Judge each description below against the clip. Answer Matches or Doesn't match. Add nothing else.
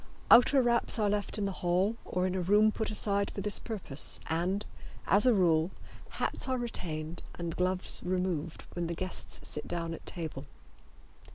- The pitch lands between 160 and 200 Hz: Matches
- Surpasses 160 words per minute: Matches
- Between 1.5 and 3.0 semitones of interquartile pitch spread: Doesn't match